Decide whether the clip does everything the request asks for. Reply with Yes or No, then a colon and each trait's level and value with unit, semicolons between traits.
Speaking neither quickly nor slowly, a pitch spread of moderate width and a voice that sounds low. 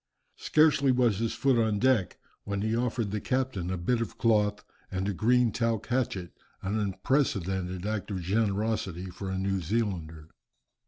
Yes: average, 160 wpm; average, 3.7 semitones; low, 105 Hz